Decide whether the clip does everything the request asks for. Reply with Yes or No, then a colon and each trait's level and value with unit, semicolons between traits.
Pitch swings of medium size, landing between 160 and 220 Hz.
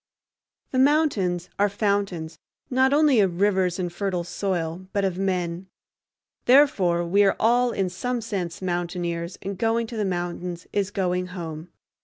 Yes: average, 3.2 semitones; high, 190 Hz